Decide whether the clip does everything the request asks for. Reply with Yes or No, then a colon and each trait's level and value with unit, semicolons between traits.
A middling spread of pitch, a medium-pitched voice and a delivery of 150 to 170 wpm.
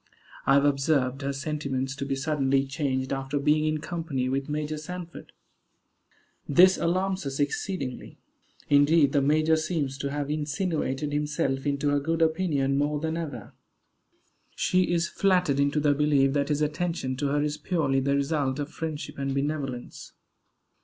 No: narrow, 2.3 semitones; medium, 145 Hz; average, 155 wpm